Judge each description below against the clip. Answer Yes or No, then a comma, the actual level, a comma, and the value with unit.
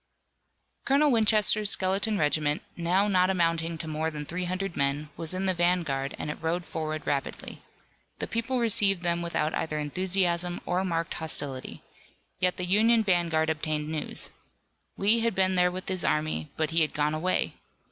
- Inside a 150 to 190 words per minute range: Yes, average, 165 wpm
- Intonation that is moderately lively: Yes, average, 3.4 semitones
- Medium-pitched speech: Yes, medium, 175 Hz